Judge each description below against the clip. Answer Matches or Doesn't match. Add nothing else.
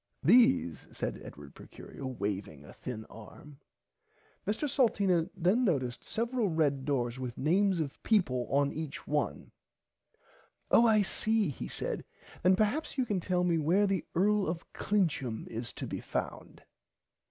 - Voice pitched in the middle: Matches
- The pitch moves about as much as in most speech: Doesn't match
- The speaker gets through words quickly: Doesn't match